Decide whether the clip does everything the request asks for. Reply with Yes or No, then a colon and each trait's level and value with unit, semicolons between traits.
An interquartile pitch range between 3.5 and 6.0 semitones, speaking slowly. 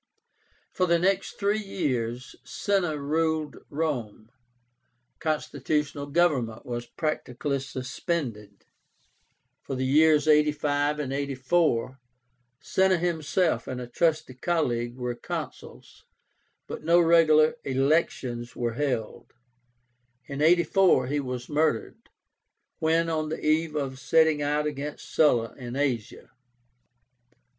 Yes: average, 4.0 semitones; slow, 105 wpm